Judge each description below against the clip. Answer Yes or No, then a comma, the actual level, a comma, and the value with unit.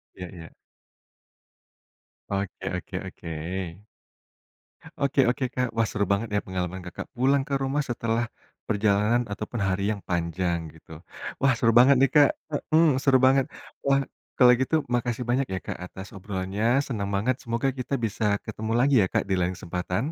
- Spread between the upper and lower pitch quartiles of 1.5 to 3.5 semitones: No, average, 5.2 semitones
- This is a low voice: Yes, low, 115 Hz